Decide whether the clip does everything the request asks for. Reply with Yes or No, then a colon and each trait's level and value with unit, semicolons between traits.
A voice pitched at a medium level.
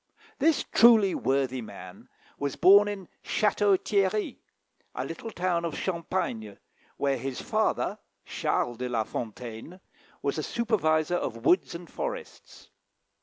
Yes: medium, 170 Hz